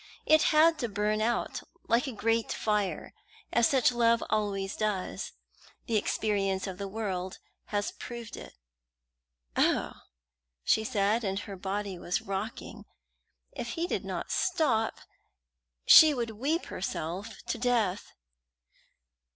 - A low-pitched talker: No, high, 215 Hz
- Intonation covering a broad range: No, average, 3.2 semitones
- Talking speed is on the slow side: Yes, slow, 125 wpm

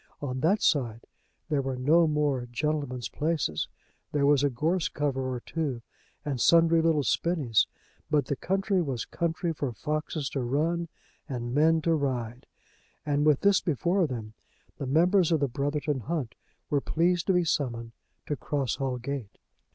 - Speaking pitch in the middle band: Yes, medium, 145 Hz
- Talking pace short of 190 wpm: Yes, average, 165 wpm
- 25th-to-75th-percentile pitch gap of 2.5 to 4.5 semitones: Yes, average, 4.0 semitones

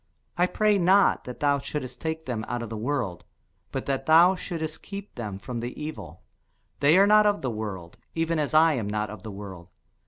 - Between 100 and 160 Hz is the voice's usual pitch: Yes, medium, 140 Hz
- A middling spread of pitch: No, wide, 7.3 semitones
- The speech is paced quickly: Yes, fast, 210 wpm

